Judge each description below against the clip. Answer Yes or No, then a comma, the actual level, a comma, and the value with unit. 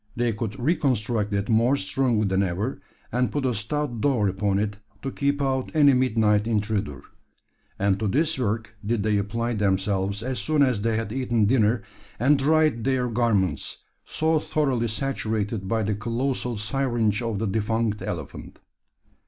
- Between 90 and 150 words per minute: No, average, 160 wpm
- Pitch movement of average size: Yes, average, 4.0 semitones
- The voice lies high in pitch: No, low, 115 Hz